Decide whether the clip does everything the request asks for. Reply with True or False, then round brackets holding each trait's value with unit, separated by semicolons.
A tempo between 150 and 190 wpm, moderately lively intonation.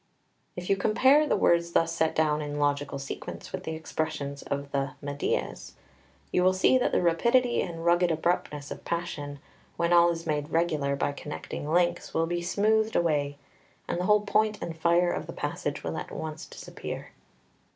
True (180 wpm; 3.3 semitones)